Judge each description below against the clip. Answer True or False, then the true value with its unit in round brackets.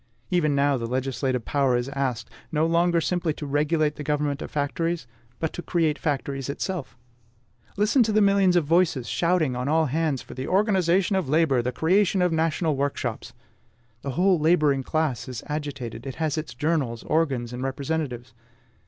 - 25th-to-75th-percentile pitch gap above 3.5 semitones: True (4.0 semitones)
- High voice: False (150 Hz)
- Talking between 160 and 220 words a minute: True (170 wpm)